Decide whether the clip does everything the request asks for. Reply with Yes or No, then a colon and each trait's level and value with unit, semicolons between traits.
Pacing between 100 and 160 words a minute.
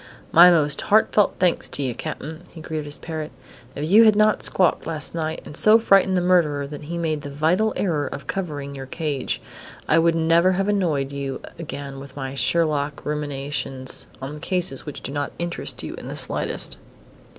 No: average, 185 wpm